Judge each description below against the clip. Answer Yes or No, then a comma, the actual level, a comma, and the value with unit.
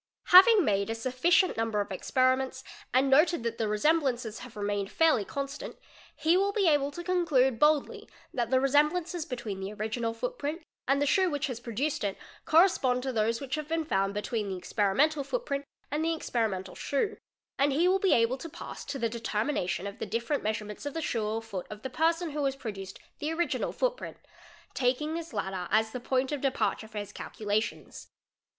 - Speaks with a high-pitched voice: Yes, very high, 260 Hz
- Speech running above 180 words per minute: Yes, average, 195 wpm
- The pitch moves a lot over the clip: Yes, wide, 6.0 semitones